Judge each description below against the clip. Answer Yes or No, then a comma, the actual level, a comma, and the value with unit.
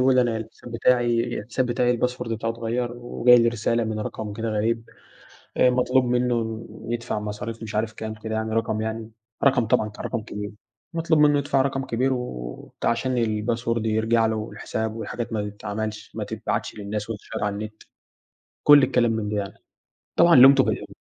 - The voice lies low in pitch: Yes, low, 115 Hz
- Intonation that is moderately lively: No, narrow, 2.2 semitones